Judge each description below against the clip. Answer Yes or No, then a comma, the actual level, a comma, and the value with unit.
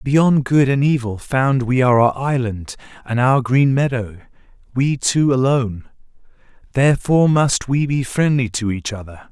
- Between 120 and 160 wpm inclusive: Yes, average, 140 wpm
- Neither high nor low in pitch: No, low, 130 Hz